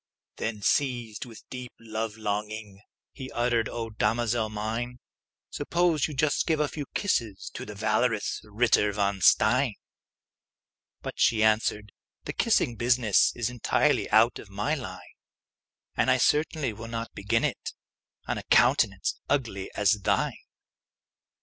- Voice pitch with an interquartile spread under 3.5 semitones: Yes, average, 2.9 semitones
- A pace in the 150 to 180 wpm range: No, average, 140 wpm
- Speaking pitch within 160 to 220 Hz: No, low, 115 Hz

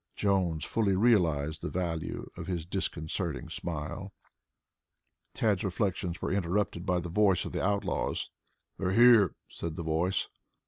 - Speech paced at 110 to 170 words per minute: Yes, average, 145 wpm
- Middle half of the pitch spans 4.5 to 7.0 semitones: No, average, 3.2 semitones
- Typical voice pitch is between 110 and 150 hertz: No, very low, 90 Hz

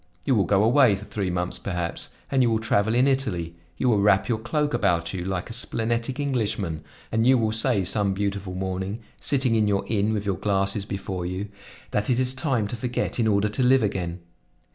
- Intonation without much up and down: No, average, 3.8 semitones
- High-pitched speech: No, low, 105 Hz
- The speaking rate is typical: No, fast, 210 wpm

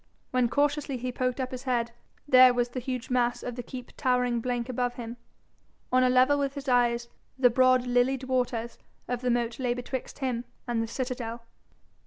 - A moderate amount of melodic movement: No, narrow, 1.2 semitones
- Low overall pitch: No, very high, 250 Hz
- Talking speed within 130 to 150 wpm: No, average, 190 wpm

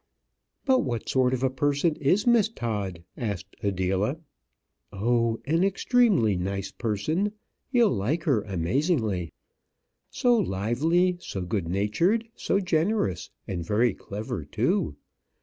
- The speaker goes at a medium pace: No, slow, 120 wpm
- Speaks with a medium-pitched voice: No, low, 120 Hz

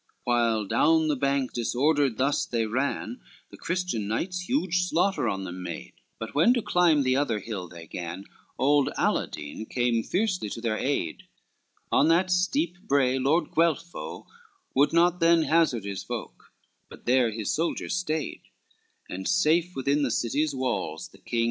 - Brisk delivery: No, average, 160 wpm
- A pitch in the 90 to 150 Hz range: Yes, medium, 140 Hz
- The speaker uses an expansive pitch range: Yes, wide, 6.8 semitones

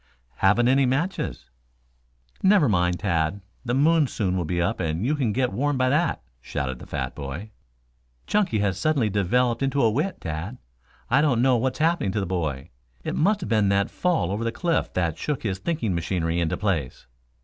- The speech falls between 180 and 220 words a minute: Yes, average, 190 wpm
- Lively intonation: Yes, wide, 7.7 semitones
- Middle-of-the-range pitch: No, low, 110 Hz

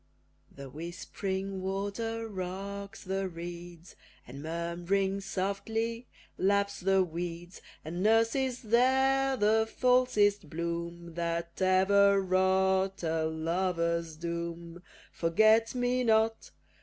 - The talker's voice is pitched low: No, high, 190 Hz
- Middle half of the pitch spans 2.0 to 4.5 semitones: Yes, average, 4.2 semitones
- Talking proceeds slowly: Yes, slow, 95 wpm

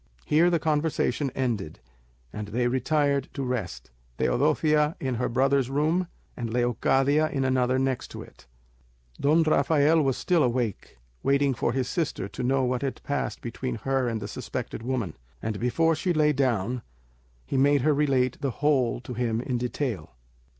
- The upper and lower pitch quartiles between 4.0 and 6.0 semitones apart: No, average, 3.3 semitones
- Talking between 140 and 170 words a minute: Yes, average, 160 wpm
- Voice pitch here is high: No, low, 130 Hz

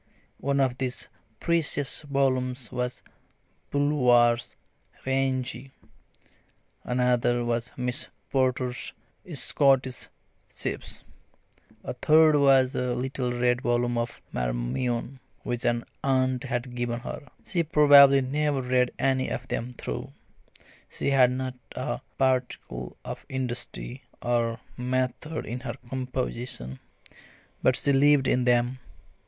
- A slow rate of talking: Yes, slow, 110 wpm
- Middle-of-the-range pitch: No, low, 125 Hz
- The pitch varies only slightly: Yes, narrow, 1.7 semitones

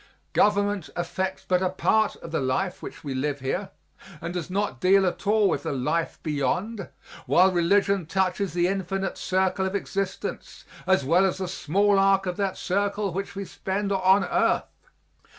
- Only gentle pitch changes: Yes, narrow, 2.1 semitones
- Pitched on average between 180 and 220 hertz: Yes, high, 190 Hz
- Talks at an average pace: Yes, average, 170 wpm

